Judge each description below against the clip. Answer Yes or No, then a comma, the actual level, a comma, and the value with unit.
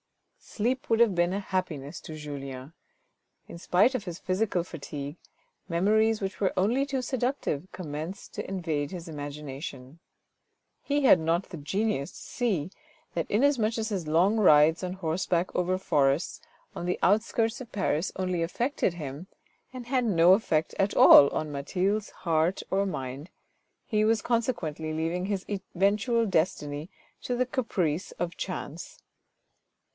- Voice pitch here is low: No, medium, 185 Hz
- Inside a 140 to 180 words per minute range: Yes, average, 145 wpm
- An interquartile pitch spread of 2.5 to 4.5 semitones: No, wide, 5.5 semitones